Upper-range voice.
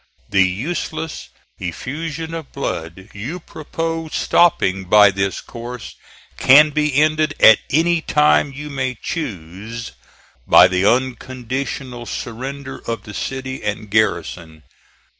No: low, 130 Hz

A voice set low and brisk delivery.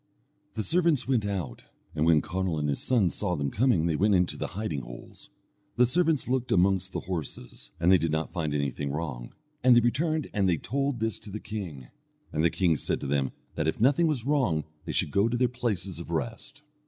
Yes: very low, 95 Hz; fast, 215 wpm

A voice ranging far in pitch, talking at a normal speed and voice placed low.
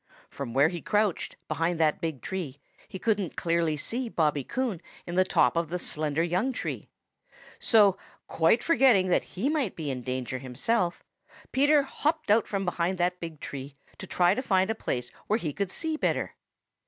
No: wide, 5.9 semitones; average, 180 wpm; medium, 180 Hz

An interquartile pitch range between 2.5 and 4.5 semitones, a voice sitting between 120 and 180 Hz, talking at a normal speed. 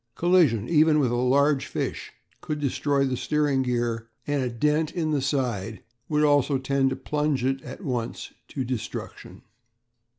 Yes: average, 3.0 semitones; low, 135 Hz; average, 160 wpm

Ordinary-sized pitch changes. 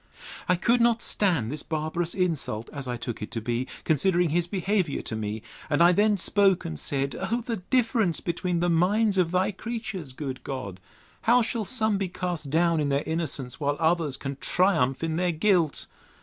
No: wide, 5.7 semitones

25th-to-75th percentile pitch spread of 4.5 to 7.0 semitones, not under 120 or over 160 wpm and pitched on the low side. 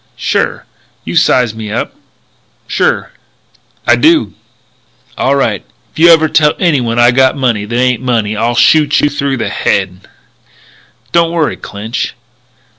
Yes: average, 5.1 semitones; slow, 135 wpm; low, 125 Hz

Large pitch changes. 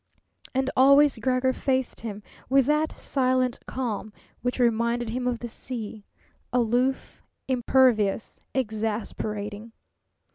No: average, 2.8 semitones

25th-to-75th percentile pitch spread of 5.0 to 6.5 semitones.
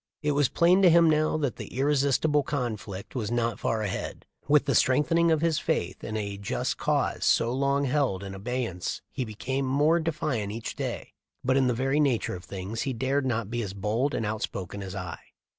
Yes: wide, 5.4 semitones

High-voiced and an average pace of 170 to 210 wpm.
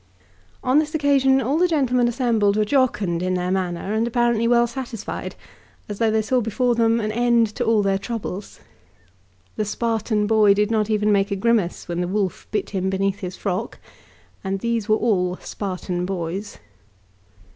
Yes: high, 215 Hz; average, 175 wpm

